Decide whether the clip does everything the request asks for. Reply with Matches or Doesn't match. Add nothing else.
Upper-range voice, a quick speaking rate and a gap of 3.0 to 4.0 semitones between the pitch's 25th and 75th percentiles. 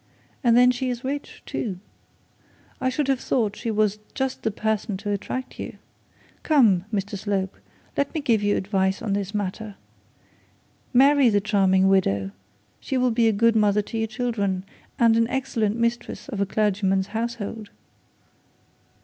Doesn't match